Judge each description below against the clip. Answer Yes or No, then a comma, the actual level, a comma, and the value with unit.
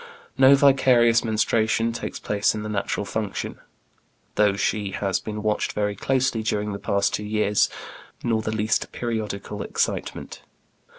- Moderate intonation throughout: No, narrow, 1.8 semitones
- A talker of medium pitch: No, low, 110 Hz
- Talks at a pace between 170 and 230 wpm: No, average, 150 wpm